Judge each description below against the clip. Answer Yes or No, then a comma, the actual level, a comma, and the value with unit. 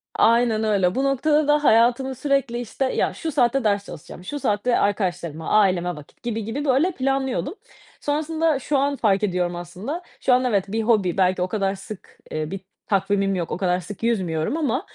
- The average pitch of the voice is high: Yes, high, 220 Hz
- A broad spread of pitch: Yes, wide, 6.2 semitones